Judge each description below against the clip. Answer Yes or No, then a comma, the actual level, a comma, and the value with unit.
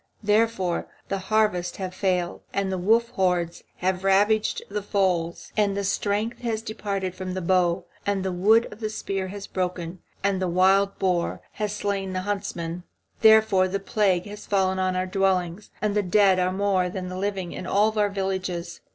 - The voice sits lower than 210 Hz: Yes, high, 190 Hz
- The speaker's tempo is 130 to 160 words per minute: No, average, 180 wpm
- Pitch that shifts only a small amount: Yes, narrow, 2.0 semitones